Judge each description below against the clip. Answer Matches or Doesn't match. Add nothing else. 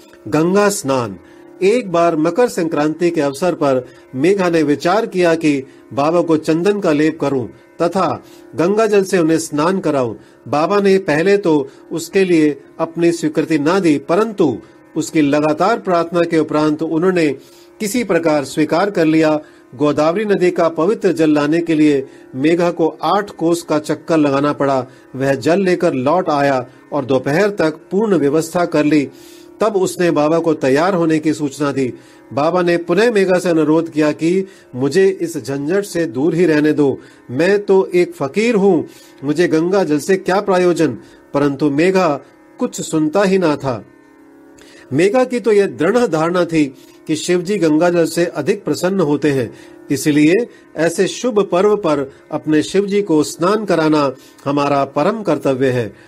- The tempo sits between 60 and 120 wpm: Doesn't match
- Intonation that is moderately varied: Matches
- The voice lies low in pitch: Doesn't match